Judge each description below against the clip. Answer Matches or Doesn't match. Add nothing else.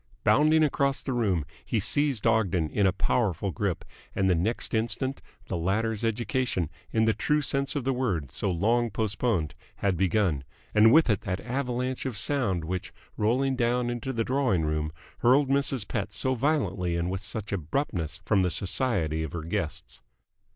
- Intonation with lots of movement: Matches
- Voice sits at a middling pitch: Doesn't match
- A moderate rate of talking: Matches